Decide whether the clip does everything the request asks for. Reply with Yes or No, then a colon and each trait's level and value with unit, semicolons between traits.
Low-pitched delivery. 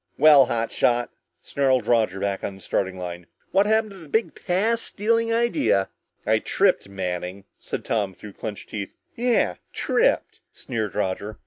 Yes: low, 115 Hz